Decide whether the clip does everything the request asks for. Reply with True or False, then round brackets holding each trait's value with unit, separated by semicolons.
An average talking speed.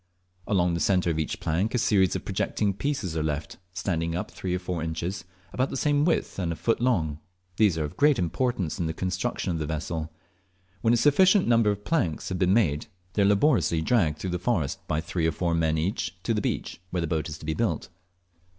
False (225 wpm)